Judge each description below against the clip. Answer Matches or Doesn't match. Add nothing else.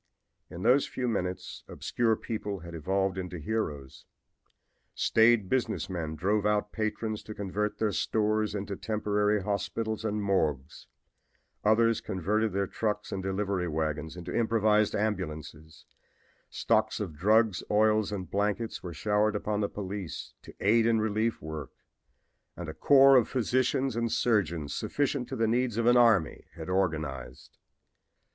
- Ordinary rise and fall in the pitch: Matches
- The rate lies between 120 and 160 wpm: Matches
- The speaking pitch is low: Matches